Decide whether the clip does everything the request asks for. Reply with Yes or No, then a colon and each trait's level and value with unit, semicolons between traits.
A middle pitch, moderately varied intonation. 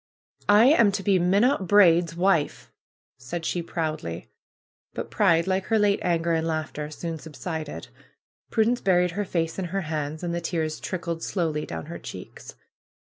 Yes: medium, 170 Hz; average, 3.3 semitones